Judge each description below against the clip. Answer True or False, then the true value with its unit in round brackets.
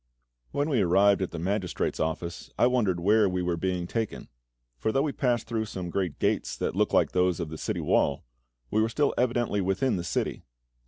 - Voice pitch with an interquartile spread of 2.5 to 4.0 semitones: False (4.5 semitones)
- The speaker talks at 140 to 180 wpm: False (205 wpm)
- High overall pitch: False (100 Hz)